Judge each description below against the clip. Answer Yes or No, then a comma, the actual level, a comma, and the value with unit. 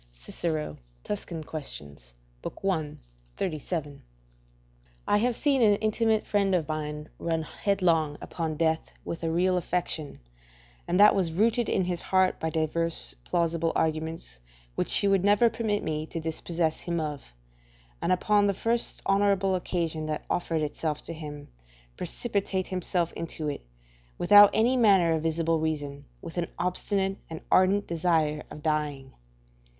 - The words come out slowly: No, average, 145 wpm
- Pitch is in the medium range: Yes, medium, 170 Hz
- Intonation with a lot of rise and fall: No, average, 3.9 semitones